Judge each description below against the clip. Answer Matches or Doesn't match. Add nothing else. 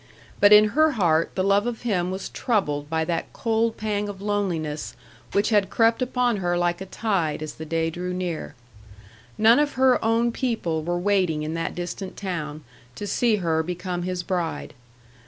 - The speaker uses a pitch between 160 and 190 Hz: Matches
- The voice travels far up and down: Doesn't match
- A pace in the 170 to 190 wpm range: Matches